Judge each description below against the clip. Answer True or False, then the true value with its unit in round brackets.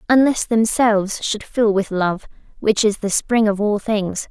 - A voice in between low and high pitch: False (210 Hz)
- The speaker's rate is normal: True (180 wpm)